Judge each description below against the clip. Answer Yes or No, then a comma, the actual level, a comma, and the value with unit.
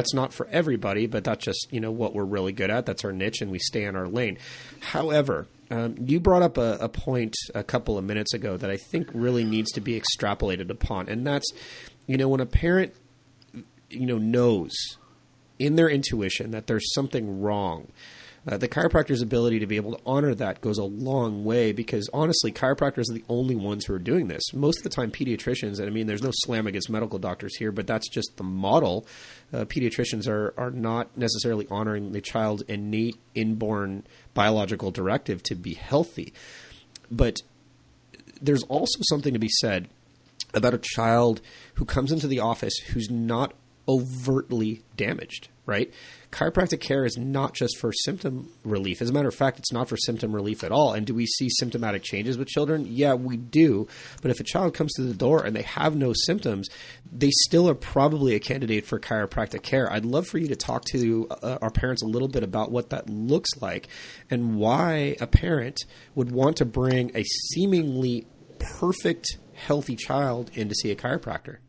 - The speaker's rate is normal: Yes, average, 195 wpm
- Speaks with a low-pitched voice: Yes, low, 120 Hz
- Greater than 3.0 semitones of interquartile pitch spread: Yes, average, 3.8 semitones